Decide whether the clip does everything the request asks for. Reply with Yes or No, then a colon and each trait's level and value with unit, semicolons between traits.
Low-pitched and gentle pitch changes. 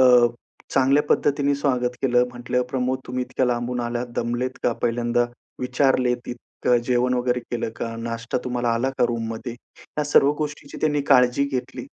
Yes: low, 125 Hz; narrow, 1.4 semitones